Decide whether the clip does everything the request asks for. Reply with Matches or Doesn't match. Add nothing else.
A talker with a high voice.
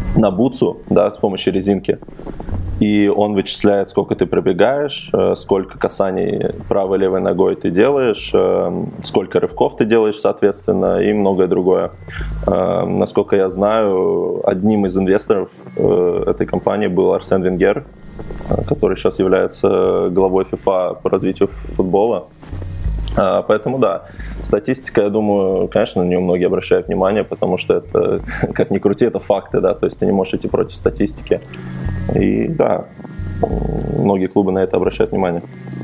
Doesn't match